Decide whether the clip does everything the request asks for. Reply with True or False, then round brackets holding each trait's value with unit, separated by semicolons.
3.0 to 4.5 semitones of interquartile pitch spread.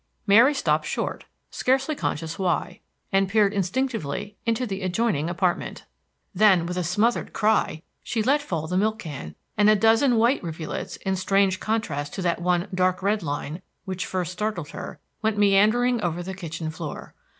True (4.0 semitones)